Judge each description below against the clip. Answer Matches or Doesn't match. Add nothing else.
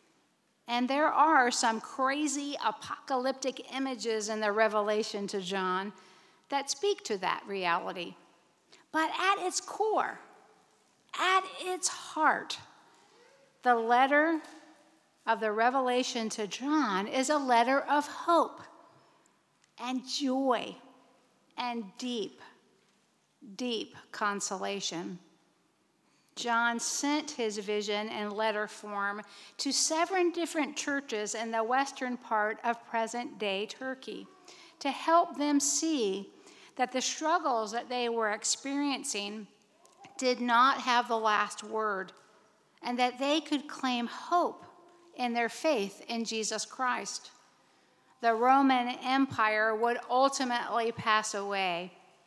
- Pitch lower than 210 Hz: Doesn't match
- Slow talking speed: Matches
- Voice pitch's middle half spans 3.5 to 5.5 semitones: Matches